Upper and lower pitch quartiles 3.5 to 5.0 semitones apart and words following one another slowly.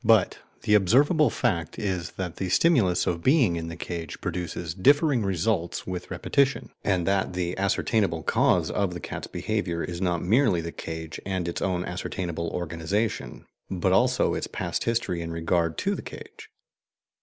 No: average, 3.8 semitones; average, 165 wpm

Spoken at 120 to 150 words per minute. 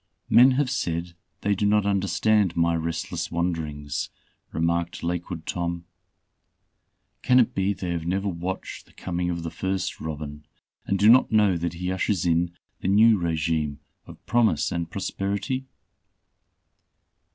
Yes: average, 140 wpm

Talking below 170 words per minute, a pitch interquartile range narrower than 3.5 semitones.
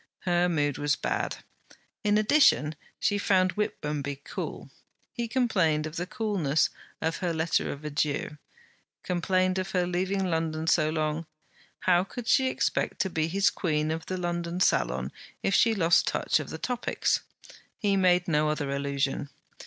No: average, 155 wpm; average, 3.9 semitones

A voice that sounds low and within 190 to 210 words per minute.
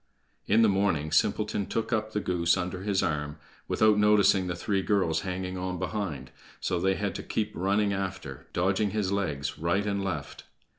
No: very low, 95 Hz; average, 180 wpm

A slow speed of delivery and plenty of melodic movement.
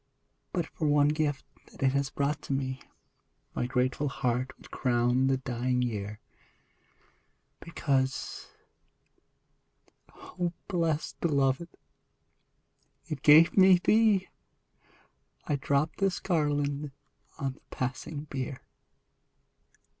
No: slow, 100 wpm; average, 3.2 semitones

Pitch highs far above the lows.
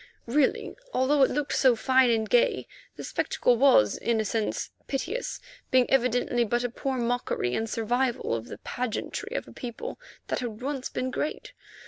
No: narrow, 2.4 semitones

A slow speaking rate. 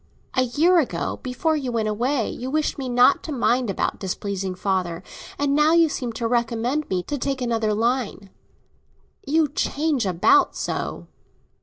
No: average, 160 wpm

